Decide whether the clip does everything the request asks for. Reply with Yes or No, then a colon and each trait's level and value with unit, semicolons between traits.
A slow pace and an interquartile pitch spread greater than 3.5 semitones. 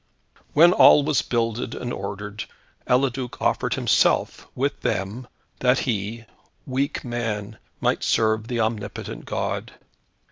No: slow, 115 wpm; average, 3.2 semitones